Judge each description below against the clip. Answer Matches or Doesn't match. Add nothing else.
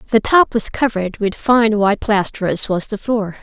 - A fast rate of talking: Matches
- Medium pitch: Doesn't match